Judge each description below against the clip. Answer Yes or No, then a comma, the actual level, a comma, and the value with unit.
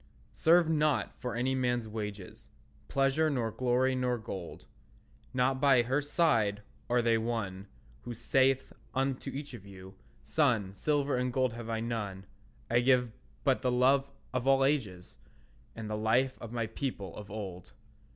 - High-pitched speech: No, low, 125 Hz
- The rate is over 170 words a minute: No, average, 155 wpm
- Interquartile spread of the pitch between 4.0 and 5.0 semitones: No, average, 3.5 semitones